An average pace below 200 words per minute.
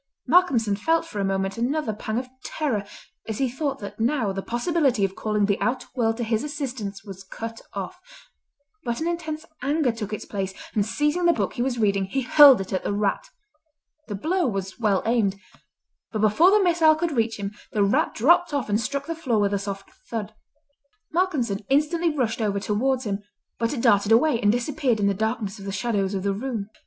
No: fast, 205 wpm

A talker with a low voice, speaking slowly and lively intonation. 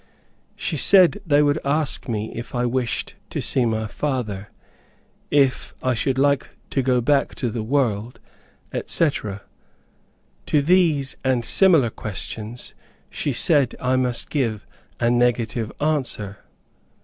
No: low, 125 Hz; slow, 130 wpm; average, 3.9 semitones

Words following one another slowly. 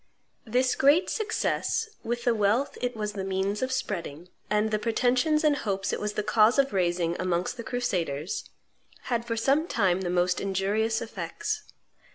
No: average, 170 wpm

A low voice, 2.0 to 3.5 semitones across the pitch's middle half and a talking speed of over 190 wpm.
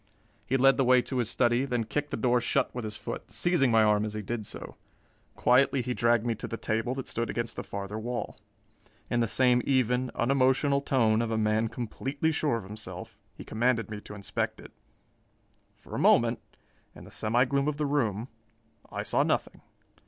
Yes: low, 120 Hz; average, 3.1 semitones; average, 200 wpm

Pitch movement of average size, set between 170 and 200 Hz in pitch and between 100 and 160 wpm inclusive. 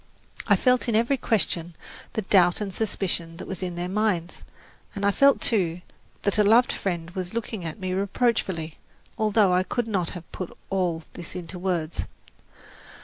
No: average, 3.6 semitones; medium, 185 Hz; average, 170 wpm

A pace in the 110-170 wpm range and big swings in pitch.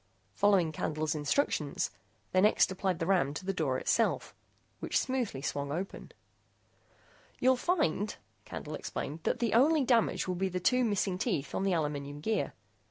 Yes: average, 160 wpm; wide, 6.5 semitones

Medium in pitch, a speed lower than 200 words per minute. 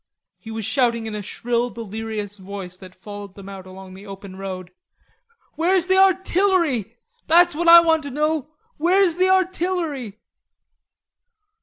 No: high, 235 Hz; average, 145 wpm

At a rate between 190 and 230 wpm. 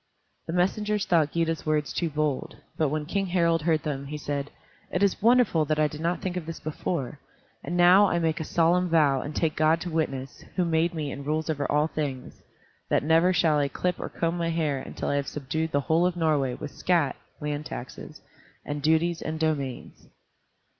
Yes: fast, 205 wpm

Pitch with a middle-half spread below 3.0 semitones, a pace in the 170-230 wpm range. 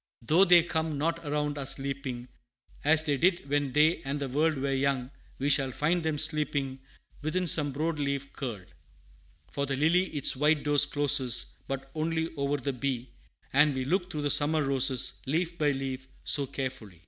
Yes: narrow, 2.6 semitones; average, 180 wpm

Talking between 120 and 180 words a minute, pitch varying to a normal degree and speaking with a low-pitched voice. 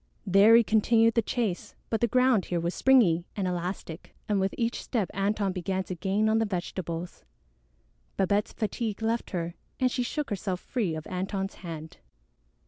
No: average, 170 wpm; average, 3.9 semitones; high, 200 Hz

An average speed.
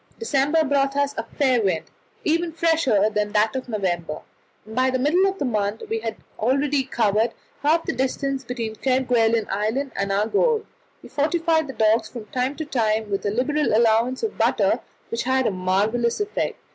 Yes: average, 185 wpm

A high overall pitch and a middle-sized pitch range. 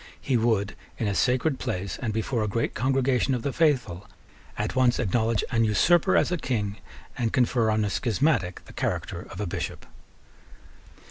No: low, 115 Hz; average, 3.6 semitones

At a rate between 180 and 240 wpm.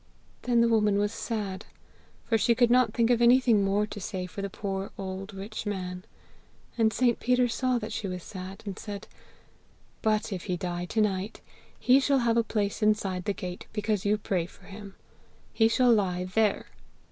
Yes: average, 190 wpm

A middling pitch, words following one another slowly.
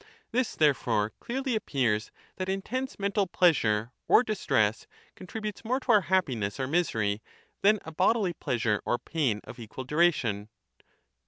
No: medium, 160 Hz; average, 150 wpm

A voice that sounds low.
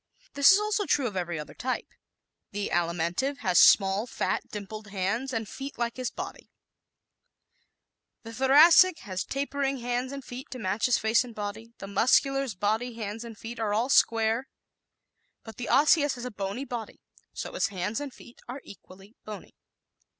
No: high, 230 Hz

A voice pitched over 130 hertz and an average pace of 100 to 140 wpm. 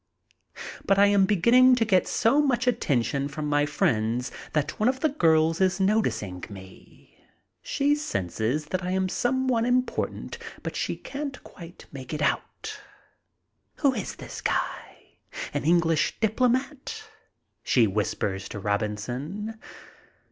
Yes: medium, 185 Hz; slow, 135 wpm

